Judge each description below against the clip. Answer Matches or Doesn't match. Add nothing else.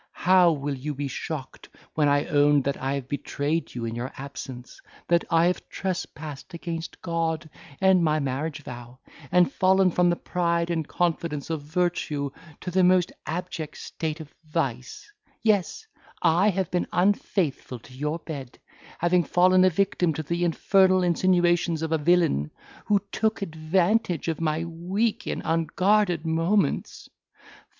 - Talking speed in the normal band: Matches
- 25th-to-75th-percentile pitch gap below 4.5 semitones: Matches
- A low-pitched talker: Doesn't match